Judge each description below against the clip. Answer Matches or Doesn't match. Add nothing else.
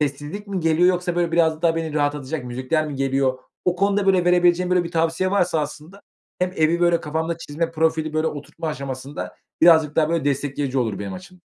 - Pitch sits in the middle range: Matches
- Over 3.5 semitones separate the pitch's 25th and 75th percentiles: Doesn't match